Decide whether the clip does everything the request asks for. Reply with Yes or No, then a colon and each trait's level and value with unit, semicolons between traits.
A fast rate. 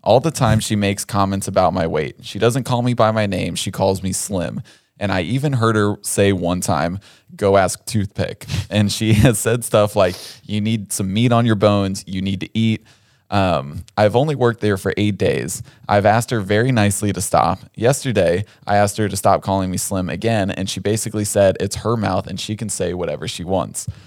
Yes: fast, 215 wpm